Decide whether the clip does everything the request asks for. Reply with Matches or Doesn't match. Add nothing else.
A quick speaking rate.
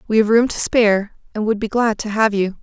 Matches